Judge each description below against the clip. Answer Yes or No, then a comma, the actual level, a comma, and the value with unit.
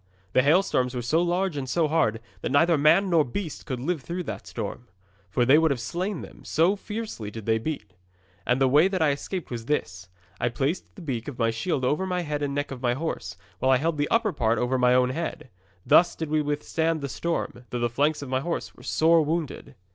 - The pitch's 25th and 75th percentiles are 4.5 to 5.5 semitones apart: Yes, average, 5.0 semitones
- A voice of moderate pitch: Yes, medium, 145 Hz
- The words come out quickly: Yes, fast, 230 wpm